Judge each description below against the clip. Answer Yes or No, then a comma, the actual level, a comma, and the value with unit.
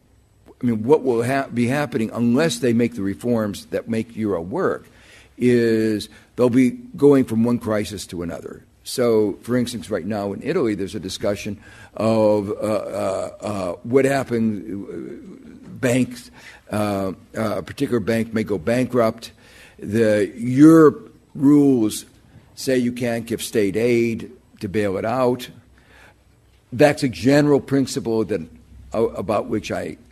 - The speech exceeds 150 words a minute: No, average, 140 wpm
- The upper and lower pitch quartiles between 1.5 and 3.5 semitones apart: Yes, average, 3.0 semitones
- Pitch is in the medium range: No, low, 115 Hz